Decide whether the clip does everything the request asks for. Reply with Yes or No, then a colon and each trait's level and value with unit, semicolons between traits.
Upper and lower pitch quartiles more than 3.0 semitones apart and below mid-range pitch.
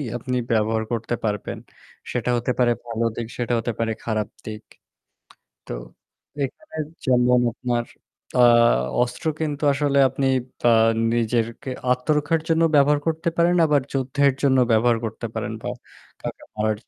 Yes: average, 3.6 semitones; low, 125 Hz